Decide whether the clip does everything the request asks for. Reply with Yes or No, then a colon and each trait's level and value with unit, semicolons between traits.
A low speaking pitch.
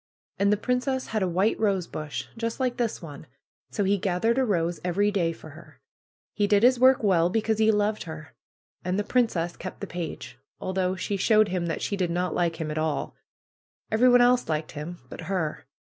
No: high, 195 Hz